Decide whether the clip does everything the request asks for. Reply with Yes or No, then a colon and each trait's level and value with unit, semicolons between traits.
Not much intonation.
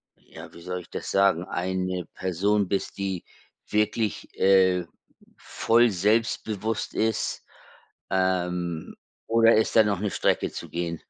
No: average, 3.0 semitones